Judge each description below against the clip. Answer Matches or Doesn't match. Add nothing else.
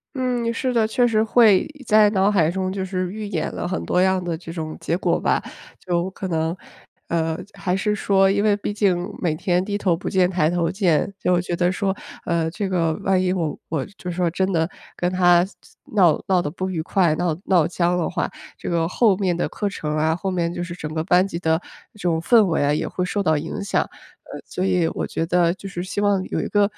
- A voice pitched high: Doesn't match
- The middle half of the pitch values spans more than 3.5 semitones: Doesn't match